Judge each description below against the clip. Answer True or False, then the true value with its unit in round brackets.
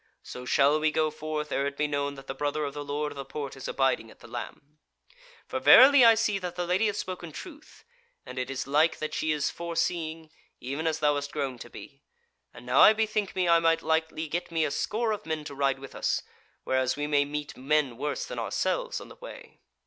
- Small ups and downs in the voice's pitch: False (3.4 semitones)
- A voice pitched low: False (150 Hz)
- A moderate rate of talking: False (235 wpm)